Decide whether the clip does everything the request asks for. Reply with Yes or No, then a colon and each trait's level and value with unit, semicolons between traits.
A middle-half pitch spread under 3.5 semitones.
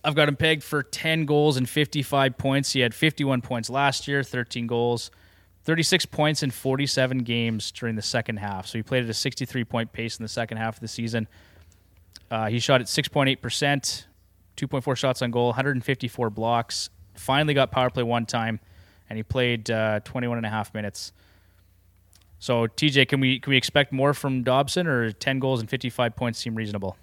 No: average, 3.8 semitones